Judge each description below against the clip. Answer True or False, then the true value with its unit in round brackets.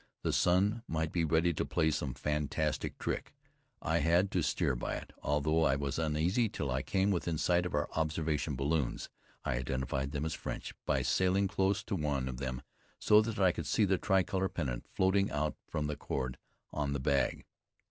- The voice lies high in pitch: False (80 Hz)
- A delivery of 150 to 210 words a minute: True (190 wpm)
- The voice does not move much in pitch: False (4.5 semitones)